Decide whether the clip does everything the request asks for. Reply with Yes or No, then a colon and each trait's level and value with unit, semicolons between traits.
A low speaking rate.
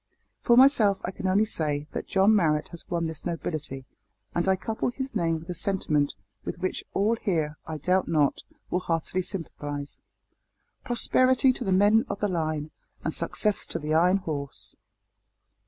No: average, 170 wpm